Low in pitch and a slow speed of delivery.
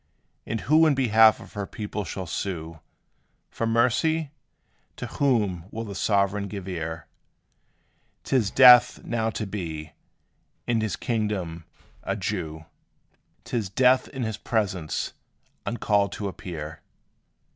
Yes: low, 105 Hz; slow, 130 wpm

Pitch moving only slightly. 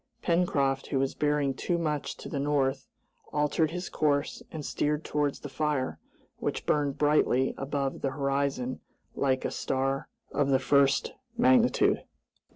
Yes: narrow, 1.8 semitones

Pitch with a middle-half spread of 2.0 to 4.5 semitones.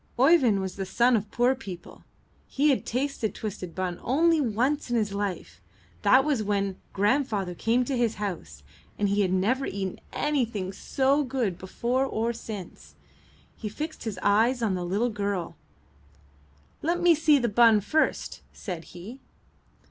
No: average, 5.2 semitones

